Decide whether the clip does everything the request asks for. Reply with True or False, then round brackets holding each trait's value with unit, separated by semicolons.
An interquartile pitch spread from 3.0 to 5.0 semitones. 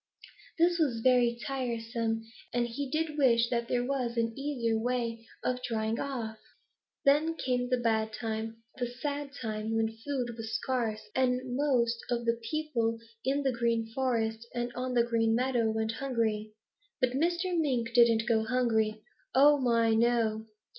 False (2.5 semitones)